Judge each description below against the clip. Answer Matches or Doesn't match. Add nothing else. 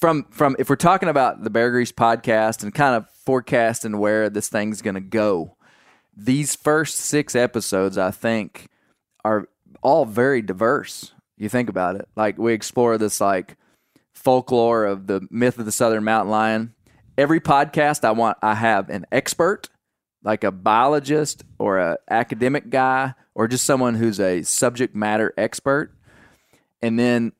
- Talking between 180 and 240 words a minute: Doesn't match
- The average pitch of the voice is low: Matches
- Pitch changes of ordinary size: Matches